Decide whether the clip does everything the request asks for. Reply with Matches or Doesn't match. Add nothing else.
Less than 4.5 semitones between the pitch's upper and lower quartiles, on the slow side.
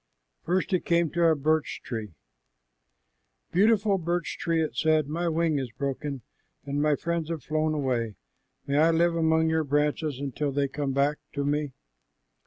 Doesn't match